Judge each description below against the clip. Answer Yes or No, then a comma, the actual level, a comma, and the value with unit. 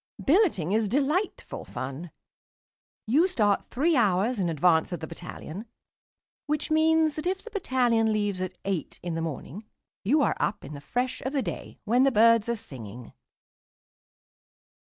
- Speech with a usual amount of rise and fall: No, wide, 7.9 semitones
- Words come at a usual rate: Yes, average, 155 wpm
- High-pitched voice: Yes, high, 220 Hz